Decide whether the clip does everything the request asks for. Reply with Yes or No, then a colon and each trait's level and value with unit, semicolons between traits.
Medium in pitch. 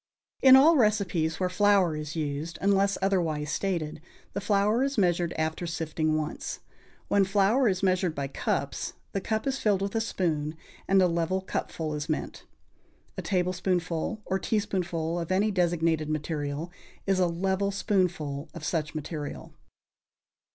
Yes: medium, 180 Hz